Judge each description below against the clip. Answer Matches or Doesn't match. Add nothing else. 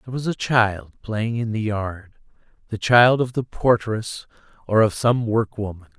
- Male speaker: Matches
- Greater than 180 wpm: Doesn't match